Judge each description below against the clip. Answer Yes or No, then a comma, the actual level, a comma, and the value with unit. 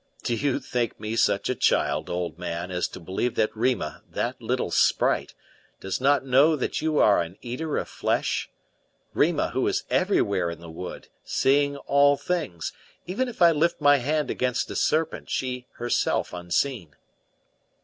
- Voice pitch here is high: No, low, 125 Hz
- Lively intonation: Yes, wide, 7.7 semitones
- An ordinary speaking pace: Yes, average, 165 wpm